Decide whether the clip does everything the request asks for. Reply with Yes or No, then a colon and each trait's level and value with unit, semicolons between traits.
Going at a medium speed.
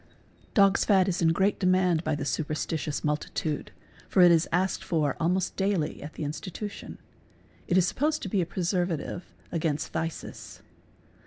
Yes: average, 160 wpm